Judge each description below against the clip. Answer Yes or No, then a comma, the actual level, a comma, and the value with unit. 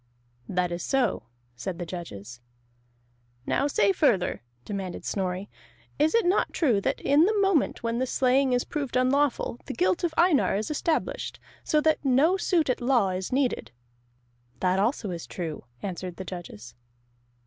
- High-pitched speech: Yes, high, 235 Hz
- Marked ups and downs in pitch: Yes, wide, 7.9 semitones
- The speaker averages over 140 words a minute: Yes, average, 160 wpm